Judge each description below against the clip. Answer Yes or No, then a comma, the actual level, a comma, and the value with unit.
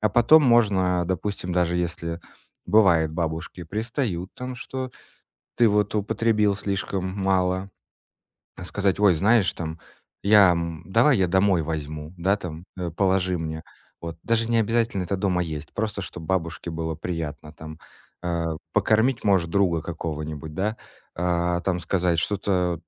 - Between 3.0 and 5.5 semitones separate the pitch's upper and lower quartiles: Yes, average, 3.6 semitones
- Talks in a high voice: No, very low, 90 Hz